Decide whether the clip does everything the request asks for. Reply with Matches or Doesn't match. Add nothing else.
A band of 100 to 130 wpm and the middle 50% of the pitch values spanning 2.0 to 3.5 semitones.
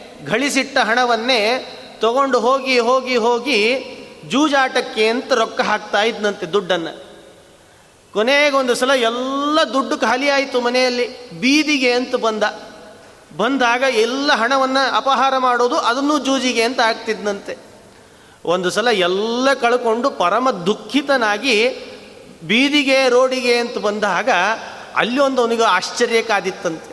Matches